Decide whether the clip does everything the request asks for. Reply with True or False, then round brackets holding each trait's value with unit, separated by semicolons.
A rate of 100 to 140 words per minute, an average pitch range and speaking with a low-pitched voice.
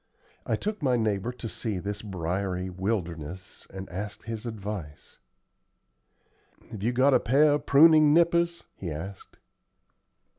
False (135 wpm; 6.0 semitones; 105 Hz)